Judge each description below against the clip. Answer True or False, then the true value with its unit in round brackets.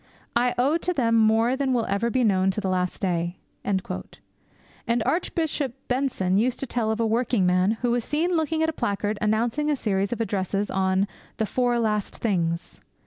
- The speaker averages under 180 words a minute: False (190 wpm)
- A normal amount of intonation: True (4.4 semitones)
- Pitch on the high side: True (225 Hz)